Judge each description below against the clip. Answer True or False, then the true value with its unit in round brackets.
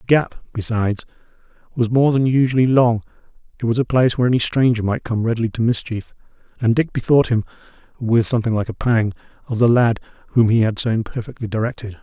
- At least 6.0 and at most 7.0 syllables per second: True (6.4 syllables/s)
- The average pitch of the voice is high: False (115 Hz)